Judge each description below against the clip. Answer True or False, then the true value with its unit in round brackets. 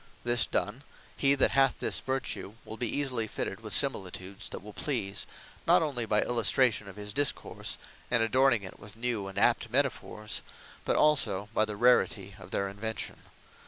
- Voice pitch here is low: True (110 Hz)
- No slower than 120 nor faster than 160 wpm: False (170 wpm)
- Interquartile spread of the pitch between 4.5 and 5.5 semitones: False (4.1 semitones)